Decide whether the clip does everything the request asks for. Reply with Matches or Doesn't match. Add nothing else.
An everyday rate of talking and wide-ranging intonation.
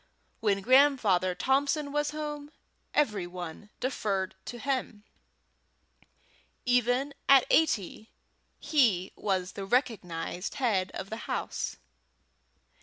Doesn't match